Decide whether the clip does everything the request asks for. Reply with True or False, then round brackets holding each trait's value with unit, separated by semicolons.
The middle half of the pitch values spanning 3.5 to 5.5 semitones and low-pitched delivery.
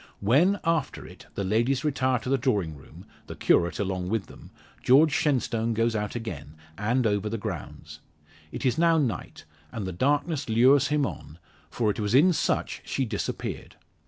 True (5.2 semitones; 115 Hz)